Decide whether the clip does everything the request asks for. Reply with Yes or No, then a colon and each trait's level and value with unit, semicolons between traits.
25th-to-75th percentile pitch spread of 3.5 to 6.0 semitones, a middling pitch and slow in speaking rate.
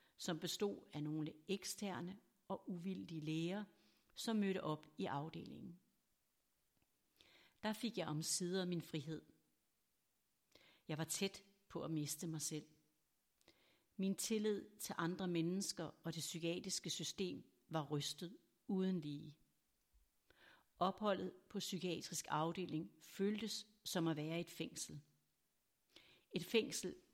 Yes: average, 3.9 semitones; medium, 170 Hz; slow, 115 wpm